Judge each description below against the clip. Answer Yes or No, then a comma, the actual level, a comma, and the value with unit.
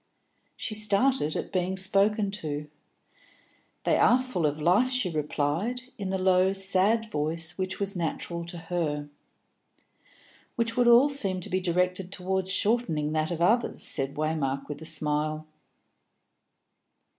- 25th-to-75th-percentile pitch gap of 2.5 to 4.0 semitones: No, average, 4.6 semitones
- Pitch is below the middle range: No, medium, 185 Hz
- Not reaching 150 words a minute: Yes, average, 140 wpm